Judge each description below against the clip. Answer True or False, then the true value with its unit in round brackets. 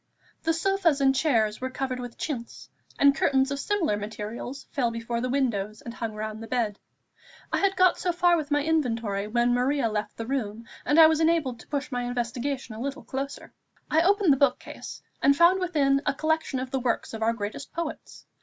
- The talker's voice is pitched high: True (265 Hz)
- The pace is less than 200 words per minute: False (205 wpm)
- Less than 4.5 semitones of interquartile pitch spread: False (4.8 semitones)